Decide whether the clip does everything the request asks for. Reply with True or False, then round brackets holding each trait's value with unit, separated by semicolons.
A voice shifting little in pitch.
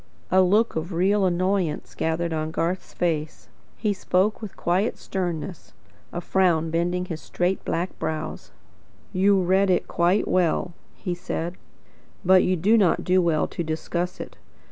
True (2.1 semitones)